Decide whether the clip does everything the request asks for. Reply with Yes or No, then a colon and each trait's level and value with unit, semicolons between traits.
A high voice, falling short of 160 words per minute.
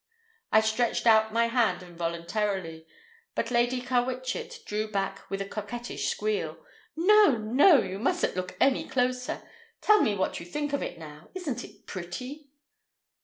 Yes: high, 230 Hz; average, 150 wpm